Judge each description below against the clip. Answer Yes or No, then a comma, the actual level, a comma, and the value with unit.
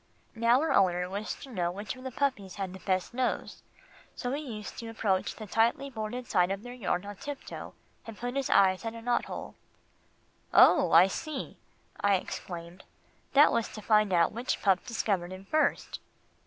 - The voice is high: Yes, high, 215 Hz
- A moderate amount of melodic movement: Yes, average, 4.5 semitones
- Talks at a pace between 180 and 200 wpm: Yes, average, 185 wpm